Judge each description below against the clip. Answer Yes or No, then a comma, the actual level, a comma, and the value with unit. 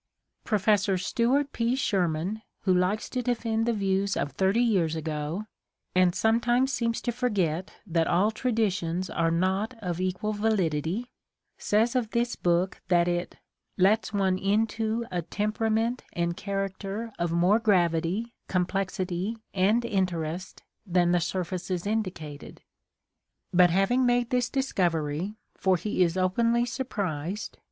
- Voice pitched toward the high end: Yes, high, 195 Hz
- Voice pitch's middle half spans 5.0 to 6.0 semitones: No, average, 4.3 semitones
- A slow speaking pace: Yes, slow, 130 wpm